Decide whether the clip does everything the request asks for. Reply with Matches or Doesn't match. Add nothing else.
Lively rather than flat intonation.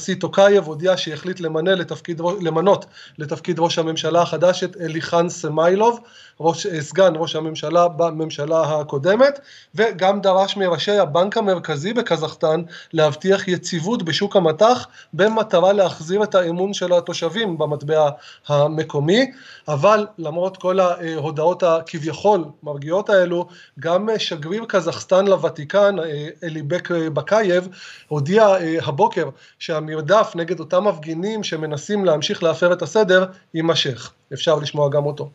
Doesn't match